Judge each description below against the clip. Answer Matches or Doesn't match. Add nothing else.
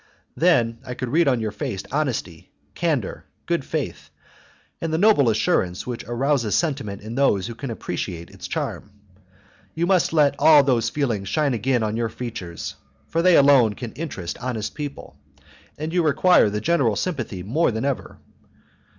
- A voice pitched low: Matches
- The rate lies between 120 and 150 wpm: Doesn't match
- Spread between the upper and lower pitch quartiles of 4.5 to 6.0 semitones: Matches